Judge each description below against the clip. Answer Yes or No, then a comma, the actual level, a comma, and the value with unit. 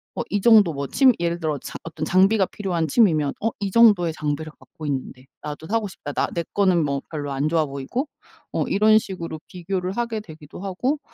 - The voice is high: No, medium, 170 Hz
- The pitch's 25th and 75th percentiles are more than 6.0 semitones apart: No, average, 5.1 semitones